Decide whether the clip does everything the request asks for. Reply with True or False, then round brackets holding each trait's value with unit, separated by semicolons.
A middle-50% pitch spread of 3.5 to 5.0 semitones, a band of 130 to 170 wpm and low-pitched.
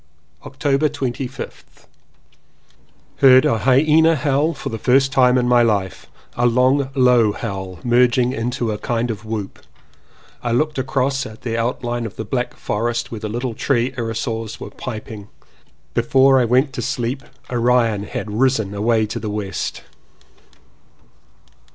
False (2.9 semitones; 150 wpm; 120 Hz)